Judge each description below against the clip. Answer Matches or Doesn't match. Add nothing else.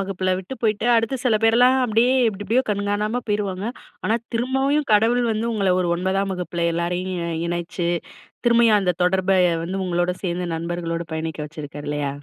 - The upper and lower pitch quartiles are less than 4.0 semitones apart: Doesn't match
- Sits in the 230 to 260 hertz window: Doesn't match